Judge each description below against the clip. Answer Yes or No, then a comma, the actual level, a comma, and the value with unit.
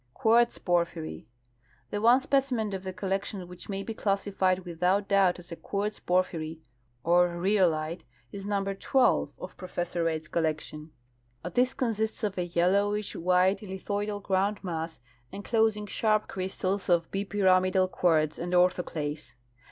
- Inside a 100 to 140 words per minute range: Yes, slow, 135 wpm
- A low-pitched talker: No, high, 190 Hz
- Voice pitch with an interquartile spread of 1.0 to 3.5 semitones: Yes, average, 2.8 semitones